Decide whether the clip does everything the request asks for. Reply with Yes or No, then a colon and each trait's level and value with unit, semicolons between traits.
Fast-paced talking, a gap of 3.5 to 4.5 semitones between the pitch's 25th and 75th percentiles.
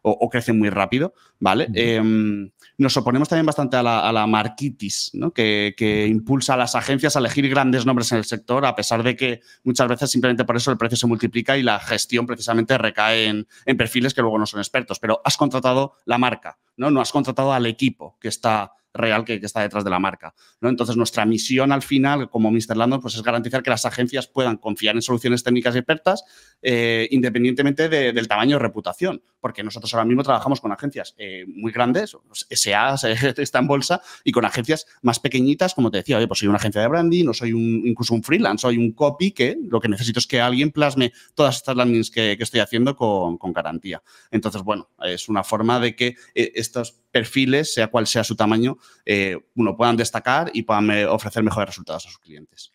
No: fast, 215 wpm; average, 2.9 semitones